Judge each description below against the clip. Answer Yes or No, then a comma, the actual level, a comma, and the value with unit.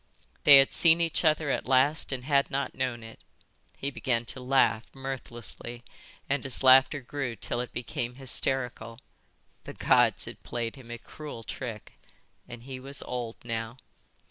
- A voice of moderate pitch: No, low, 130 Hz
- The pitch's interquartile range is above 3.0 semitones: No, narrow, 2.5 semitones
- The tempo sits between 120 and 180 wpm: Yes, average, 160 wpm